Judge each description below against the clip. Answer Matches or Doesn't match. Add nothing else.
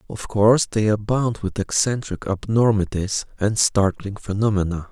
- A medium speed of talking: Doesn't match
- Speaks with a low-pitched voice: Matches